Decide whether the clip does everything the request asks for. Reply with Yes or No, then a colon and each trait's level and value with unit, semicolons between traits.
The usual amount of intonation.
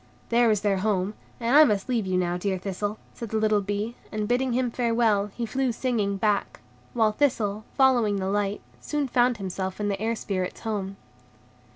Yes: average, 3.1 semitones